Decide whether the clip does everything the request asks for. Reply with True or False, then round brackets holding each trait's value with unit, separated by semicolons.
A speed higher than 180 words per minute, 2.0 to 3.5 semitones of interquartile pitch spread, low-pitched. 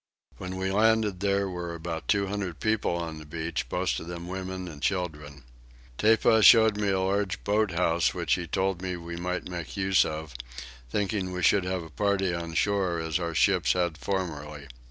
True (190 wpm; 2.9 semitones; 90 Hz)